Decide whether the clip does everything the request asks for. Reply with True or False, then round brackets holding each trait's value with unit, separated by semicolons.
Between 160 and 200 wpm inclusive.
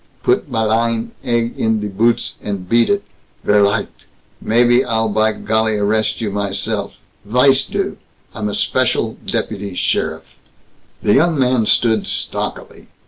False (140 wpm)